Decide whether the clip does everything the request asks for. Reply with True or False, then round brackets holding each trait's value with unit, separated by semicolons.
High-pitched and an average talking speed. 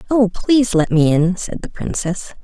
True (200 Hz; 195 wpm)